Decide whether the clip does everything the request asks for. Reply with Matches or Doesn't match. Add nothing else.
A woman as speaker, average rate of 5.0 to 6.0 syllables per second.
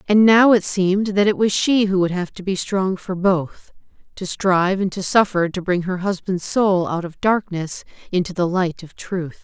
Doesn't match